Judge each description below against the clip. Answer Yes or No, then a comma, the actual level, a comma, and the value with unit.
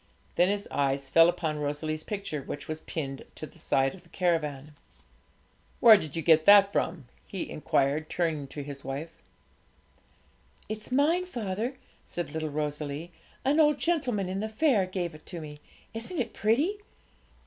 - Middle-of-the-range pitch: Yes, medium, 170 Hz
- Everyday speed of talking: Yes, average, 160 wpm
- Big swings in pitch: Yes, wide, 6.3 semitones